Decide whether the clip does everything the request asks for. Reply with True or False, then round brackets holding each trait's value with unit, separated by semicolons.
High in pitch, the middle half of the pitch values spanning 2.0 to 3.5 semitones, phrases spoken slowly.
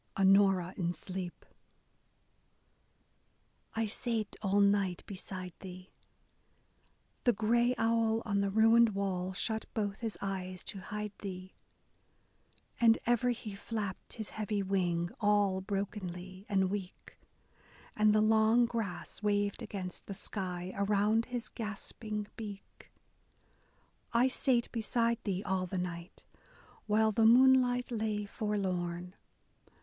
True (205 Hz; 2.9 semitones; 120 wpm)